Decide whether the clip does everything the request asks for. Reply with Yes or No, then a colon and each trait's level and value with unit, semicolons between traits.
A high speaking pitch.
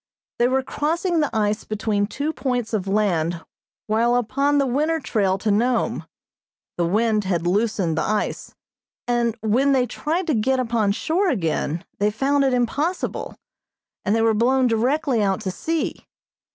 Yes: high, 235 Hz